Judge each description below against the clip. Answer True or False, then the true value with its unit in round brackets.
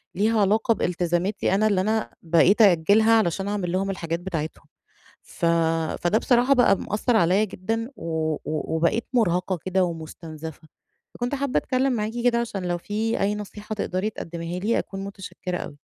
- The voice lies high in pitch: True (195 Hz)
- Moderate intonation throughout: True (4.1 semitones)